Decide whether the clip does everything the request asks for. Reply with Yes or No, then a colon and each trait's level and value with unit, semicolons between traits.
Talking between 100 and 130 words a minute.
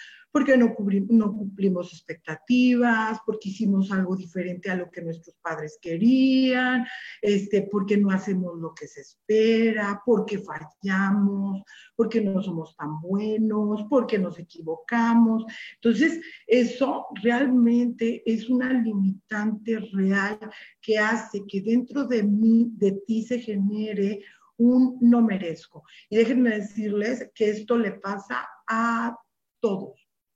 Yes: slow, 125 wpm